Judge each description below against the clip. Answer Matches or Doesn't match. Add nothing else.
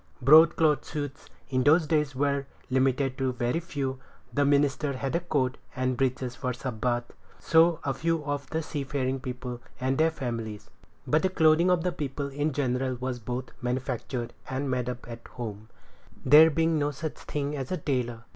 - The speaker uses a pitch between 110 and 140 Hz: Matches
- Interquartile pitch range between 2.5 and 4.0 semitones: Matches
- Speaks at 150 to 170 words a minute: Doesn't match